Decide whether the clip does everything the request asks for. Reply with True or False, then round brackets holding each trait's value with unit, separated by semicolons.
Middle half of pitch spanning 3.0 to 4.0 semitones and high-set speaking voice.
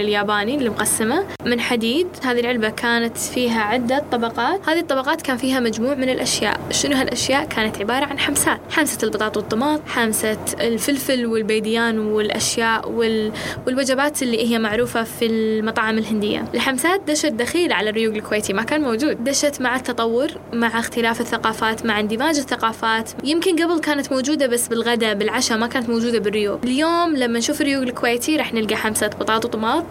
True (3.6 semitones; 235 Hz)